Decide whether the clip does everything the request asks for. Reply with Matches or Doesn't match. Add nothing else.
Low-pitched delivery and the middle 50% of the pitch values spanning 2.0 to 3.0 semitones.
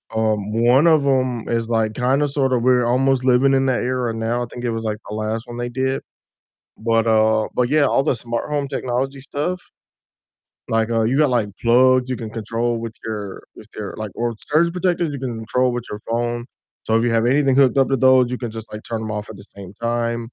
Matches